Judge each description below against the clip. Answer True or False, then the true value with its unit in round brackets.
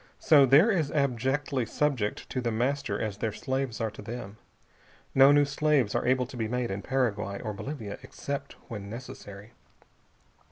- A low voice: True (125 Hz)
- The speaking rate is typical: True (160 wpm)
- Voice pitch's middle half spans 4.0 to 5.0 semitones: True (4.5 semitones)